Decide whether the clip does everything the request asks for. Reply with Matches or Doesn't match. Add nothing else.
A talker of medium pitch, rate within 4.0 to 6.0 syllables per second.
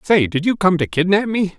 Matches